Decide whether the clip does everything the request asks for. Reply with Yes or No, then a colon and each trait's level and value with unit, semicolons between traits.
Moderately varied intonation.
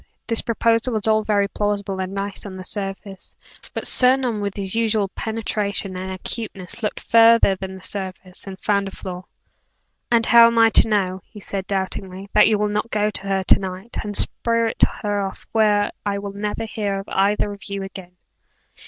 No: narrow, 2.2 semitones